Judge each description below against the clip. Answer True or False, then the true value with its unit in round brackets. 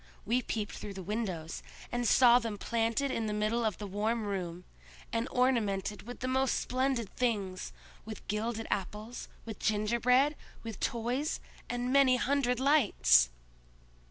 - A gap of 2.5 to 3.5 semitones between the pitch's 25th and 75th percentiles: True (3.2 semitones)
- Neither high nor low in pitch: False (230 Hz)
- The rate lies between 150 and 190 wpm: False (140 wpm)